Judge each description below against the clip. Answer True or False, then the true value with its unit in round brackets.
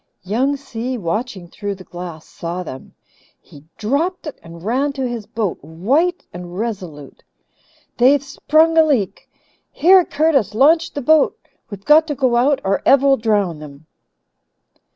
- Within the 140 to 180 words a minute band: True (150 wpm)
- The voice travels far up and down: True (7.9 semitones)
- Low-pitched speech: False (235 Hz)